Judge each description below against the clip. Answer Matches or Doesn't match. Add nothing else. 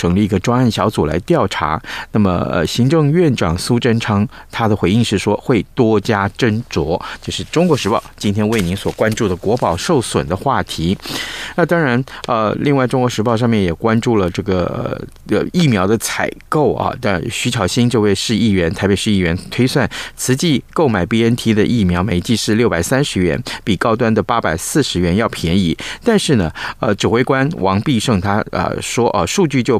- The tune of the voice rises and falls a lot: Doesn't match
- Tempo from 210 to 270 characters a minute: Doesn't match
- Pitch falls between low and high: Doesn't match